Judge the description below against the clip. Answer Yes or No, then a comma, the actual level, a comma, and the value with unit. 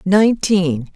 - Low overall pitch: No, medium, 185 Hz